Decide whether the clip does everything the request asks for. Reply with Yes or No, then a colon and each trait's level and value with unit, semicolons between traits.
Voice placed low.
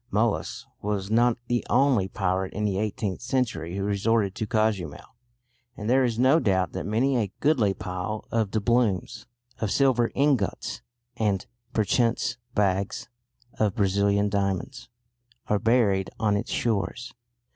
Yes: low, 105 Hz